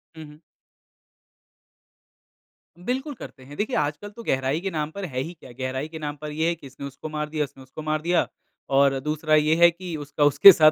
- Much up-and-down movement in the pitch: No, narrow, 2.6 semitones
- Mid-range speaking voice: Yes, medium, 155 Hz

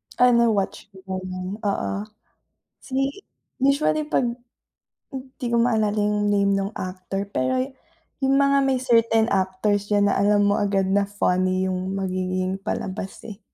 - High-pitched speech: Yes, high, 205 Hz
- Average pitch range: Yes, average, 3.7 semitones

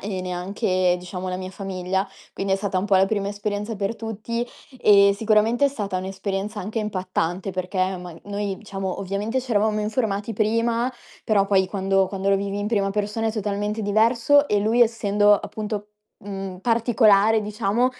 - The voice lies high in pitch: Yes, high, 205 Hz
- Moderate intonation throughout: No, narrow, 2.1 semitones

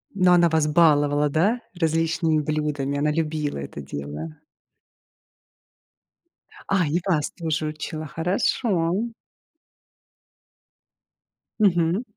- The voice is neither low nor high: Yes, medium, 155 Hz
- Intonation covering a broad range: No, average, 2.7 semitones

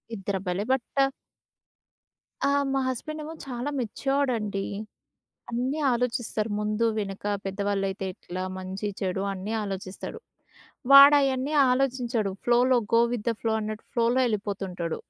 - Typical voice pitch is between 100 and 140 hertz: No, high, 220 Hz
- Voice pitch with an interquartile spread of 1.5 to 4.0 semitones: No, average, 4.4 semitones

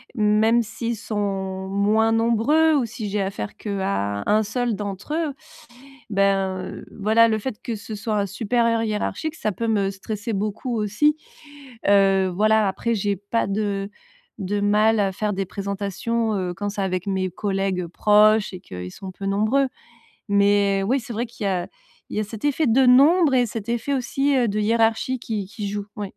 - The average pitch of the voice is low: No, high, 210 Hz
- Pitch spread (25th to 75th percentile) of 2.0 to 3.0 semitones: Yes, narrow, 2.6 semitones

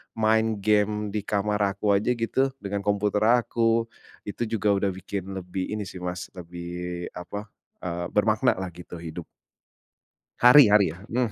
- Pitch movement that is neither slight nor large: Yes, average, 3.1 semitones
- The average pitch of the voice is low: Yes, low, 105 Hz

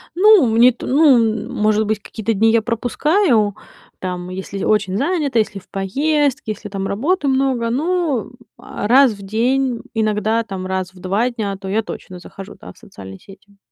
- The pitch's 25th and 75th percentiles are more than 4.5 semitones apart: Yes, average, 4.9 semitones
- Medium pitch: No, high, 220 Hz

